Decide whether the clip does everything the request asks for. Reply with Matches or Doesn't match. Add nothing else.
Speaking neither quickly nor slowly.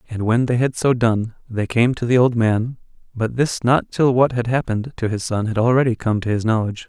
Doesn't match